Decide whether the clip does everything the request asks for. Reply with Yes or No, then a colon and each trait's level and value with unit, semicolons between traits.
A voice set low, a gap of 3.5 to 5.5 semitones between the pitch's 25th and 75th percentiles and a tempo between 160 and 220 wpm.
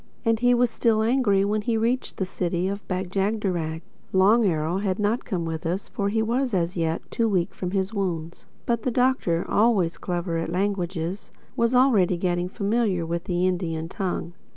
No: high, 190 Hz; average, 4.2 semitones; average, 175 wpm